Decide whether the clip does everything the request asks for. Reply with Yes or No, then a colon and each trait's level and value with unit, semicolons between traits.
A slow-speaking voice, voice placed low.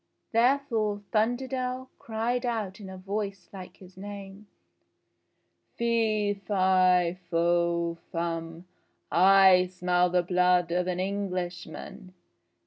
No: slow, 100 wpm; high, 190 Hz